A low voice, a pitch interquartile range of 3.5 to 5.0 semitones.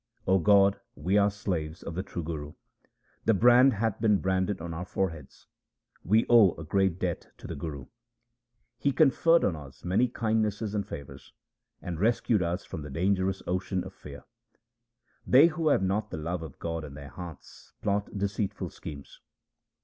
Yes: very low, 95 Hz; average, 4.3 semitones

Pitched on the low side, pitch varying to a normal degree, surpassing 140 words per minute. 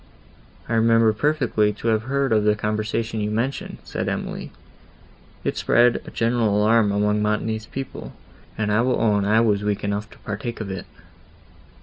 No: low, 110 Hz; narrow, 1.8 semitones; average, 170 wpm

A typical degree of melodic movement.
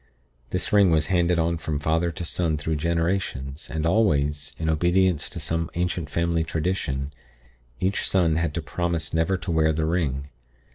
No: narrow, 2.1 semitones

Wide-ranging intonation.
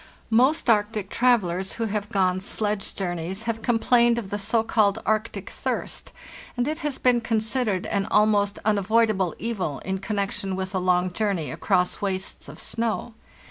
No: average, 3.2 semitones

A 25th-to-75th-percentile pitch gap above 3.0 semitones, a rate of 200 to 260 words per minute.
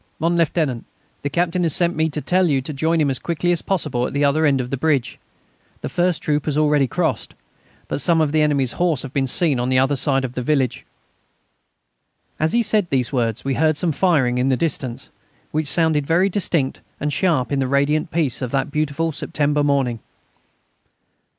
Yes: average, 3.4 semitones; fast, 205 wpm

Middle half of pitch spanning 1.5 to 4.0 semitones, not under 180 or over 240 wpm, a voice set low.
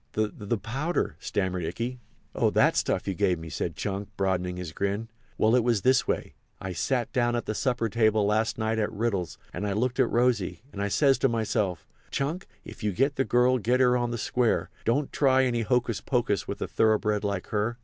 Yes: average, 3.6 semitones; average, 200 wpm; low, 110 Hz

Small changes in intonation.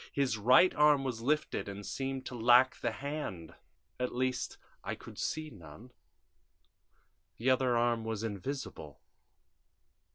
No: average, 3.3 semitones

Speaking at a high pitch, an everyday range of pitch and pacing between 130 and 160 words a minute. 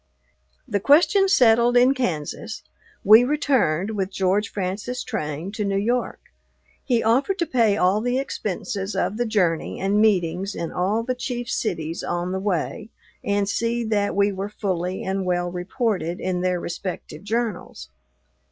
Yes: high, 205 Hz; average, 4.5 semitones; average, 150 wpm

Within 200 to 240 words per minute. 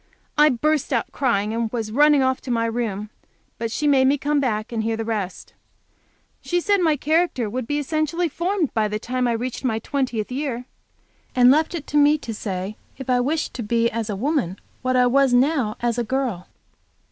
Yes: fast, 205 wpm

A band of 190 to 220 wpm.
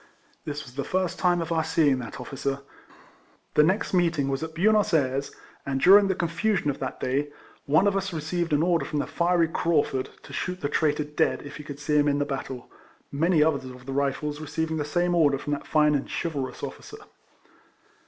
Yes: fast, 205 wpm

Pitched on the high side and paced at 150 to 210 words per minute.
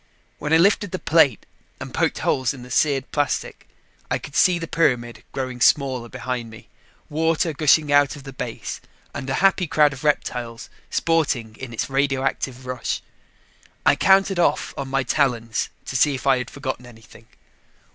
No: low, 135 Hz; average, 170 wpm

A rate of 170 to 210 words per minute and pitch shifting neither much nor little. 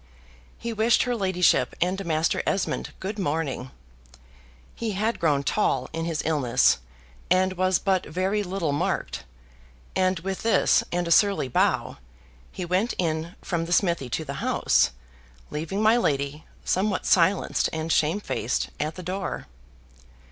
No: average, 140 wpm; average, 3.7 semitones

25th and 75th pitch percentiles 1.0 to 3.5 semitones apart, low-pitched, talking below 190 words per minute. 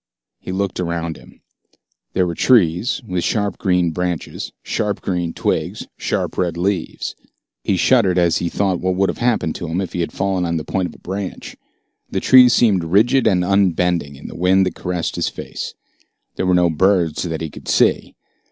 No: narrow, 2.4 semitones; very low, 90 Hz; average, 195 wpm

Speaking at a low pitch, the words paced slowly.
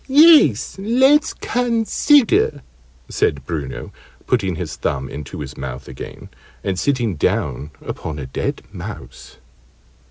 Yes: low, 105 Hz; slow, 115 wpm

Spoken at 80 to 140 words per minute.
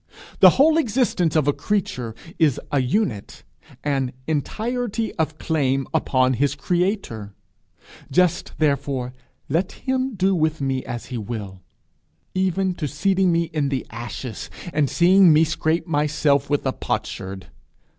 Yes: slow, 135 wpm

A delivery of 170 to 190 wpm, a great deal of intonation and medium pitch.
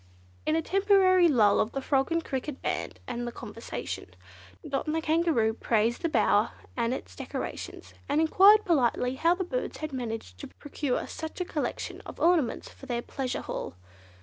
No: average, 175 wpm; wide, 5.8 semitones; very high, 285 Hz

